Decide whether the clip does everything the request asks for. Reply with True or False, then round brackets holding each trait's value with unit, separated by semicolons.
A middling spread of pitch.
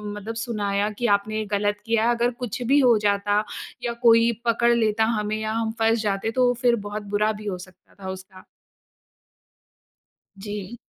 False (2.2 semitones)